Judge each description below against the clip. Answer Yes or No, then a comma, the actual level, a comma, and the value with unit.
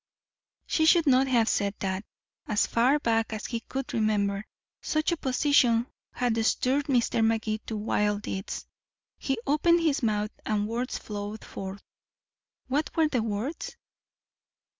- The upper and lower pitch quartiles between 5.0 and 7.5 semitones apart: No, average, 4.5 semitones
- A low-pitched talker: No, high, 230 Hz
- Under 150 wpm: Yes, average, 140 wpm